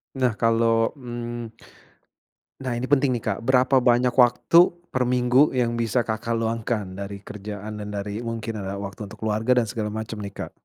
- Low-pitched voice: Yes, low, 115 Hz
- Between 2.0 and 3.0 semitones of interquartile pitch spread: Yes, average, 2.7 semitones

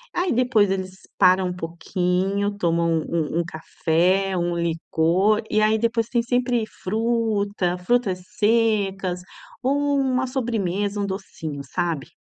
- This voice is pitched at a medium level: No, high, 195 Hz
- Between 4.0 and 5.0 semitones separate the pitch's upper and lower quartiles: Yes, average, 4.3 semitones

